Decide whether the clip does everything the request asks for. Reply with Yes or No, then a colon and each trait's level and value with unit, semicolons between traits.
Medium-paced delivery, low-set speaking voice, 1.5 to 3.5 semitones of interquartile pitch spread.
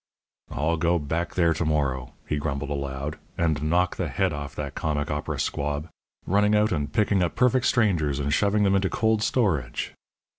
No: average, 180 wpm; very low, 80 Hz; average, 5.2 semitones